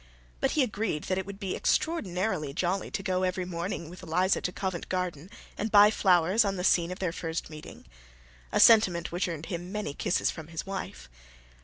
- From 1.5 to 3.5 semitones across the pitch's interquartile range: Yes, narrow, 2.6 semitones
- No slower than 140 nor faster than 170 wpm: No, average, 200 wpm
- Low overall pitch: No, medium, 185 Hz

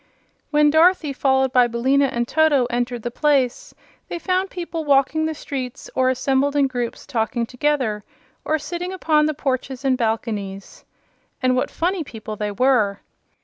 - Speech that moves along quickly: No, average, 155 wpm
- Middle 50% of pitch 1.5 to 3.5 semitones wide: No, average, 4.0 semitones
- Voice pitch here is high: Yes, very high, 265 Hz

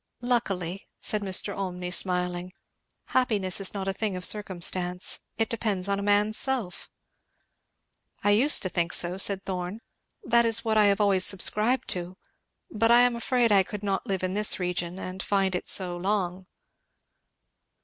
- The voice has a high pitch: Yes, high, 195 Hz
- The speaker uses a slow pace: No, average, 165 wpm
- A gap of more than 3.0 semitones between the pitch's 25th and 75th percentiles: No, average, 2.7 semitones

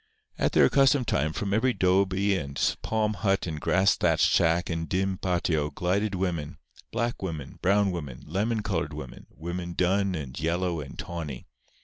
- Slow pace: No, average, 155 wpm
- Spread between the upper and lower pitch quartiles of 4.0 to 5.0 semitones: No, average, 3.4 semitones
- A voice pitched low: Yes, very low, 90 Hz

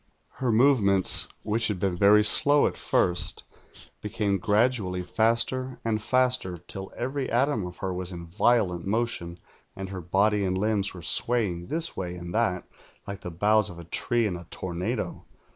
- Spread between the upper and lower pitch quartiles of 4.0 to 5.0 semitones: Yes, average, 4.4 semitones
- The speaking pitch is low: Yes, low, 100 Hz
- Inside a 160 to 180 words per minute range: Yes, average, 165 wpm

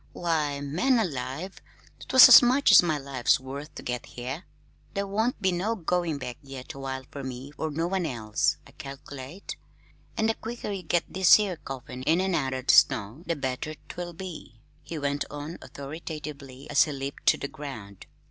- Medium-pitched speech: Yes, medium, 150 Hz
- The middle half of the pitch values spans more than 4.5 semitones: Yes, average, 5.0 semitones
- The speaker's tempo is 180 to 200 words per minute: Yes, average, 185 wpm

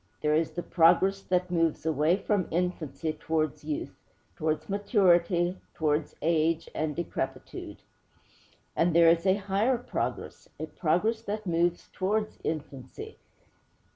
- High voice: No, medium, 170 Hz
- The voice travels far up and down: No, average, 3.4 semitones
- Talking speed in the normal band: No, slow, 125 wpm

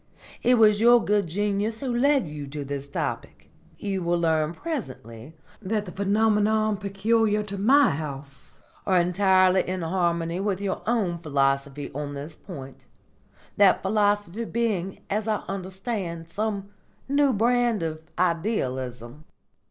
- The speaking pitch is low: No, high, 190 Hz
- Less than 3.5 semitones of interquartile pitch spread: No, average, 5.1 semitones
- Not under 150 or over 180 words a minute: No, slow, 135 wpm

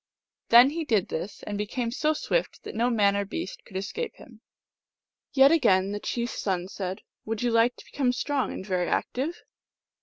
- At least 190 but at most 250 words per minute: Yes, average, 200 wpm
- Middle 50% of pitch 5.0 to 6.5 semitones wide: Yes, average, 5.3 semitones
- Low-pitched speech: No, high, 230 Hz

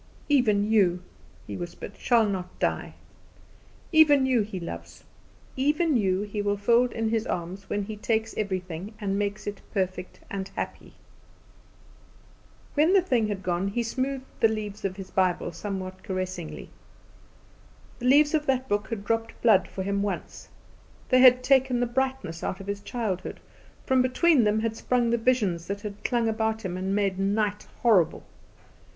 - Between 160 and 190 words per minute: Yes, average, 165 wpm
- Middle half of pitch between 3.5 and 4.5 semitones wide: Yes, average, 4.2 semitones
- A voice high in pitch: Yes, high, 210 Hz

